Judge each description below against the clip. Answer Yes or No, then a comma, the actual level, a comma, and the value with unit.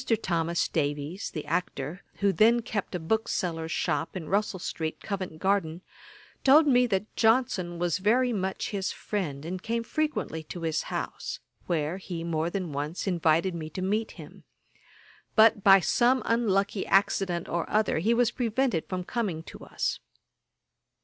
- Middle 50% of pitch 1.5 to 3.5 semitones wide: No, average, 4.8 semitones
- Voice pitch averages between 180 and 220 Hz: Yes, medium, 185 Hz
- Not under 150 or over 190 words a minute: Yes, average, 155 wpm